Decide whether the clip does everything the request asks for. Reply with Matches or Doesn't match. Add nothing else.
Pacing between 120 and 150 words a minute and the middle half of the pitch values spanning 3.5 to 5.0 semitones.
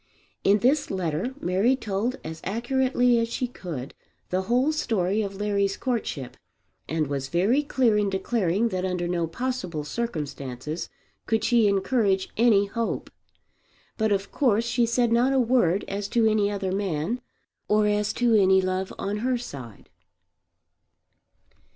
Matches